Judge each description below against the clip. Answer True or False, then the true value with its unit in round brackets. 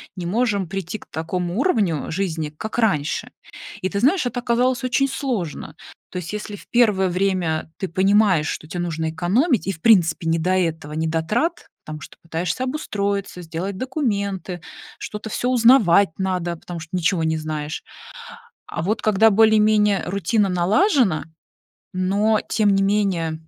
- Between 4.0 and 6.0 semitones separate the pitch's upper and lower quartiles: True (4.7 semitones)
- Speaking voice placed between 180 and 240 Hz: True (190 Hz)